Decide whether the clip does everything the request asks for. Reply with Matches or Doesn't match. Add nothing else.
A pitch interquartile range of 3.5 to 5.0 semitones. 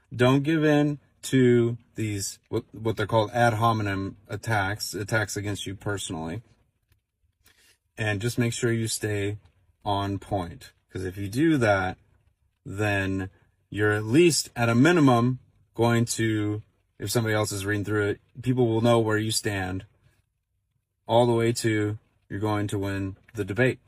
Doesn't match